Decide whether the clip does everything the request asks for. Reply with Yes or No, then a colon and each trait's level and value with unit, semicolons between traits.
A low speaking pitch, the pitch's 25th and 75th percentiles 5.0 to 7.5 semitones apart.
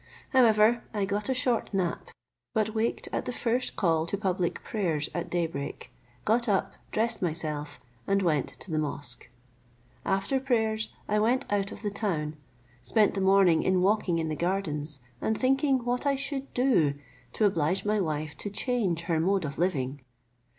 No: high, 195 Hz; wide, 5.4 semitones